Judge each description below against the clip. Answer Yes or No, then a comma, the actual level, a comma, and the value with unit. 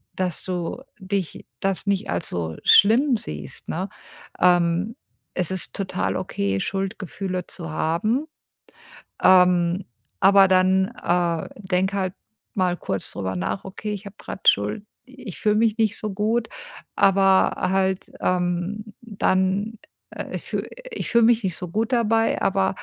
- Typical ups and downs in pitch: Yes, average, 3.0 semitones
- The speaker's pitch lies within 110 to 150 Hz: No, high, 190 Hz